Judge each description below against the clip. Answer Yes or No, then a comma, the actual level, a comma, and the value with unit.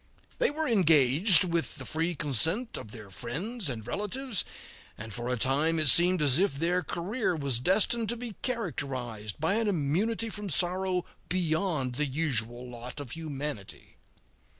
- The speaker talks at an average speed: Yes, average, 155 wpm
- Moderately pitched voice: Yes, medium, 160 Hz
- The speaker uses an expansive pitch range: Yes, wide, 6.8 semitones